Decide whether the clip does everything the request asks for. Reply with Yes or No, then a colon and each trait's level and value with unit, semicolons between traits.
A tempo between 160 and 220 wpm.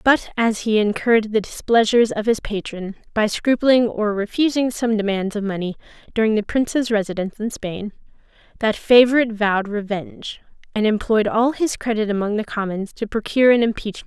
Yes: average, 180 wpm